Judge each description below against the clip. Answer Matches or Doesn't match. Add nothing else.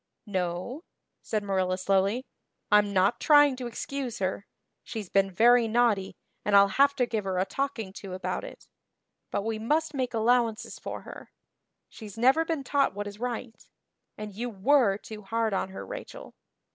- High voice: Matches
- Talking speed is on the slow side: Doesn't match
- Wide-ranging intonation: Doesn't match